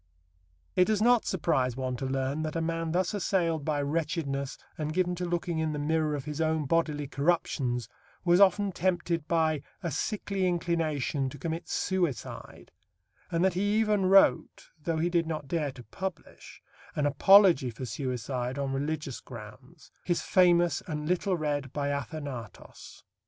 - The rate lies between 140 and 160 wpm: Yes, average, 155 wpm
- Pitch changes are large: No, average, 3.7 semitones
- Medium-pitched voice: Yes, medium, 160 Hz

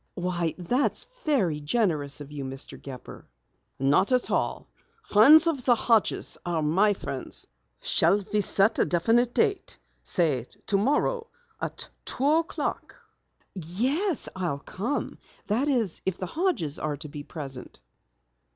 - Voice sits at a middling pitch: No, high, 195 Hz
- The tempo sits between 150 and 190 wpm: No, slow, 135 wpm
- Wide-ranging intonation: Yes, wide, 8.7 semitones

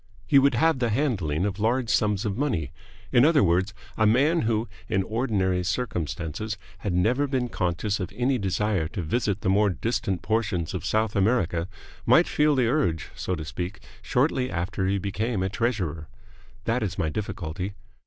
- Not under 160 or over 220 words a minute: Yes, average, 175 wpm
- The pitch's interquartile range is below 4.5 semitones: No, average, 5.0 semitones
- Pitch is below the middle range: Yes, low, 105 Hz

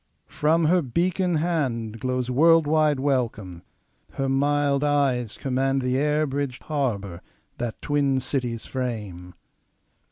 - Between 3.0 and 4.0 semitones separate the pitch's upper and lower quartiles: Yes, average, 3.4 semitones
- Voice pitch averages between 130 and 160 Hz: Yes, low, 135 Hz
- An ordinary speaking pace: No, slow, 105 wpm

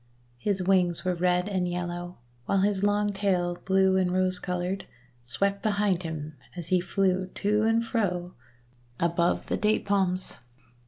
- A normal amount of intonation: No, narrow, 2.1 semitones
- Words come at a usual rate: Yes, average, 150 wpm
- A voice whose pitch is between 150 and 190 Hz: Yes, medium, 185 Hz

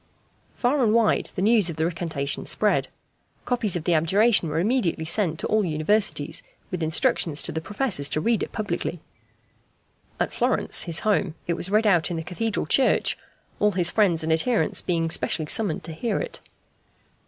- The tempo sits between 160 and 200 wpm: Yes, average, 175 wpm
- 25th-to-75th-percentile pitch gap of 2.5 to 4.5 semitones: No, average, 5.1 semitones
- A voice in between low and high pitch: Yes, medium, 180 Hz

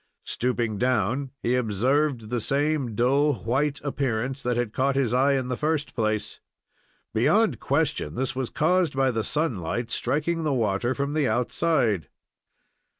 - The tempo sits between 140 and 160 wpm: Yes, average, 150 wpm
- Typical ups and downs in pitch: Yes, average, 3.6 semitones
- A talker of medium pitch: No, low, 130 Hz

